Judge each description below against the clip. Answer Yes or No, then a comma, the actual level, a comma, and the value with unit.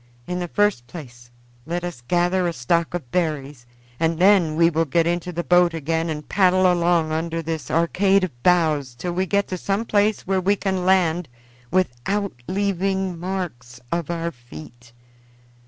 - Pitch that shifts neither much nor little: Yes, average, 3.0 semitones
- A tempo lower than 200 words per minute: Yes, average, 170 wpm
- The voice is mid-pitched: Yes, medium, 170 Hz